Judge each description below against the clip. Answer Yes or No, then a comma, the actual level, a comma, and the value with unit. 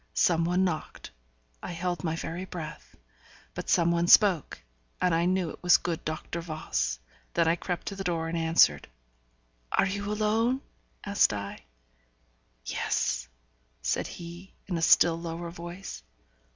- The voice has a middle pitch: Yes, medium, 170 Hz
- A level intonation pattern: Yes, narrow, 1.9 semitones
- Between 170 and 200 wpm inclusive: No, average, 150 wpm